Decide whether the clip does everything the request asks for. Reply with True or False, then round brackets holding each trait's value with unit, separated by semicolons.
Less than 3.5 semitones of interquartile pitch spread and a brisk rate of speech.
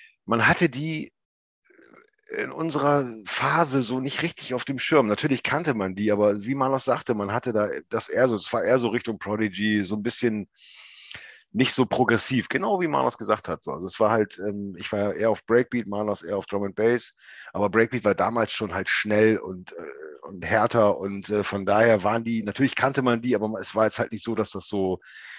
False (3.8 semitones; 205 wpm)